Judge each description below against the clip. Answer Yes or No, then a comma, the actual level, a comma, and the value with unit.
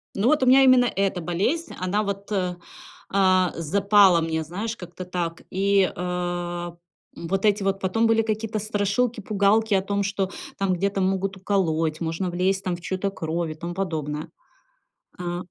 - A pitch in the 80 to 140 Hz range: No, high, 190 Hz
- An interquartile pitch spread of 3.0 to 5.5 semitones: No, narrow, 2.6 semitones